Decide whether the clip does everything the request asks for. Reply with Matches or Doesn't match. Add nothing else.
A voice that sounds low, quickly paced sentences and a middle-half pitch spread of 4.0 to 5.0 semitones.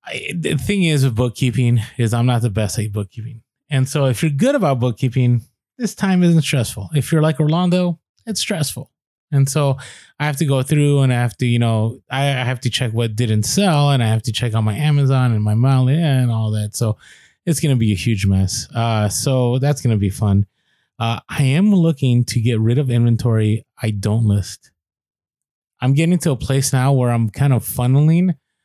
Matches